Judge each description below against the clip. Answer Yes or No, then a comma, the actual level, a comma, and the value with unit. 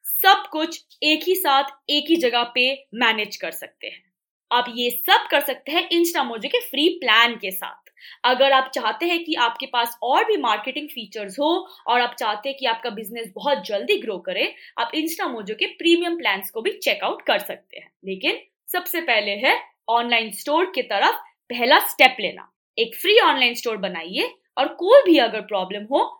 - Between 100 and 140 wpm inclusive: No, average, 185 wpm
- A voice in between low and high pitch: No, very high, 275 Hz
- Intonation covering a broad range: Yes, wide, 6.8 semitones